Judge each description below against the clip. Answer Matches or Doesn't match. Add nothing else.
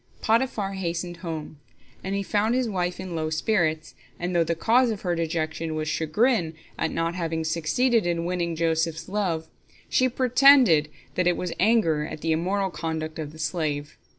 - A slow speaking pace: Doesn't match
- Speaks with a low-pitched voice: Doesn't match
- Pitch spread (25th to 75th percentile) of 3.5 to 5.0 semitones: Matches